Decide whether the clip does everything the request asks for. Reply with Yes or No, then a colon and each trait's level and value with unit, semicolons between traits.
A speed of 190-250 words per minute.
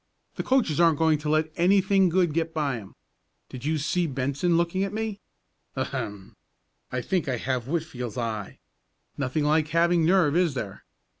No: average, 170 wpm